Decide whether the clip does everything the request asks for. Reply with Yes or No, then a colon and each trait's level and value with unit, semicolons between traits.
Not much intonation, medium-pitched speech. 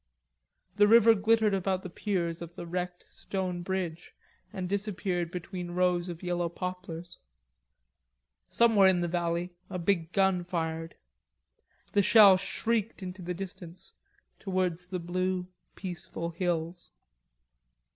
Yes: narrow, 1.9 semitones; medium, 180 Hz